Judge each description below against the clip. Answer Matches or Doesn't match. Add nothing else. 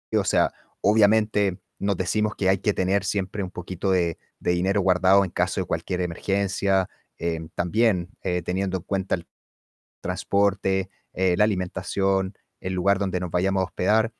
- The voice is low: Matches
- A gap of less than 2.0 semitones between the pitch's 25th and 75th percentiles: Matches